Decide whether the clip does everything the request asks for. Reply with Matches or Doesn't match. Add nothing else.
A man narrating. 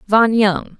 Doesn't match